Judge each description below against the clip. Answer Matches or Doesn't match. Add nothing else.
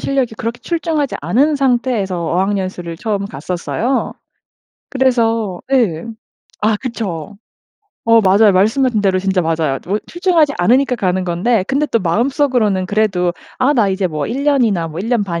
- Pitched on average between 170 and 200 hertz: Doesn't match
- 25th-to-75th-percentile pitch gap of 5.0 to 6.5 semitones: Matches